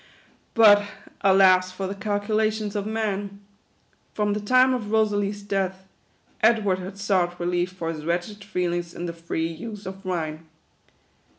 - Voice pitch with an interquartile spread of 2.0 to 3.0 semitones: Yes, average, 2.7 semitones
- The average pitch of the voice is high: Yes, high, 195 Hz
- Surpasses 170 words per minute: No, average, 140 wpm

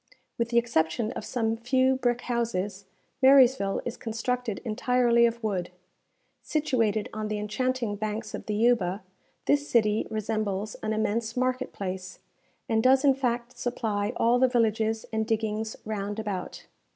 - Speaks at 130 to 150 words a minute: Yes, average, 145 wpm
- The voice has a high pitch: Yes, high, 225 Hz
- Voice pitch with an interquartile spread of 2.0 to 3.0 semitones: Yes, narrow, 2.6 semitones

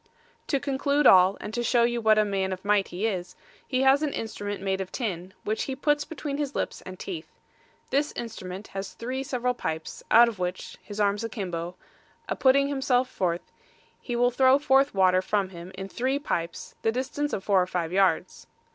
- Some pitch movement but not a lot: No, wide, 5.8 semitones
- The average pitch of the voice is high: Yes, high, 220 Hz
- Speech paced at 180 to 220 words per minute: Yes, average, 200 wpm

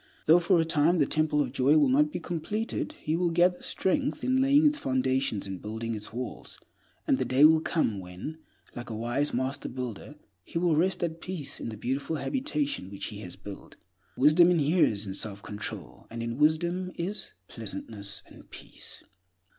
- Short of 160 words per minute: No, average, 185 wpm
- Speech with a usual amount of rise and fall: No, wide, 7.0 semitones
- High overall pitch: No, medium, 150 Hz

